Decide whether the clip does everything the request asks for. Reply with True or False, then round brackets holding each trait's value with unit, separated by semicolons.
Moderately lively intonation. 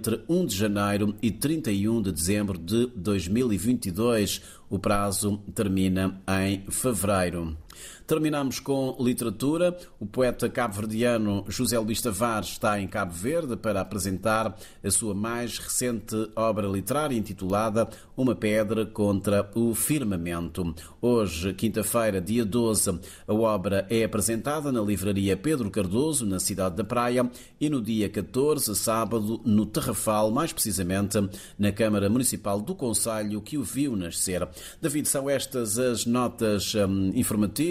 True (3.3 semitones)